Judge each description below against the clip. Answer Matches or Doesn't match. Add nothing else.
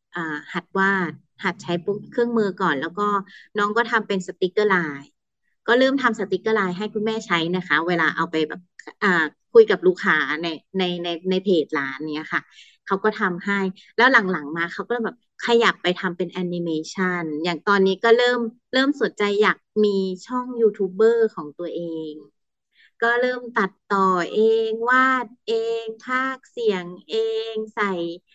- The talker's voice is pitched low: Doesn't match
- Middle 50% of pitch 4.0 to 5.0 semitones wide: Matches